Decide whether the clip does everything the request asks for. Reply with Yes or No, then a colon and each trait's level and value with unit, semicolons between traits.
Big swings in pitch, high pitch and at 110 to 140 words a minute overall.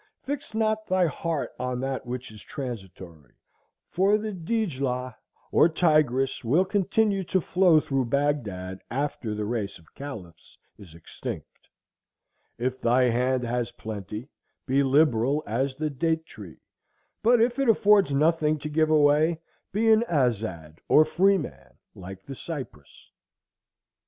No: wide, 6.3 semitones; medium, 140 Hz; slow, 135 wpm